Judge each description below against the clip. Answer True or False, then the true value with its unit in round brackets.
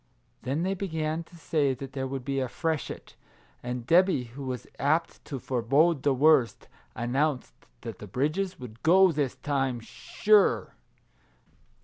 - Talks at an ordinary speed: True (145 wpm)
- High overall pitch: False (140 Hz)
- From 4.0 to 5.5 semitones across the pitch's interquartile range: True (4.3 semitones)